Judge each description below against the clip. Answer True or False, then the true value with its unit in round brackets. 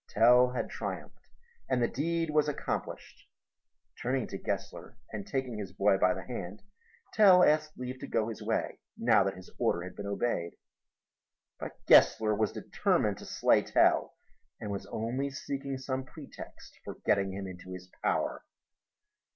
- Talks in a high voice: False (115 Hz)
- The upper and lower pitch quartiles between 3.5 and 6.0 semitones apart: True (5.3 semitones)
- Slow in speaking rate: False (160 wpm)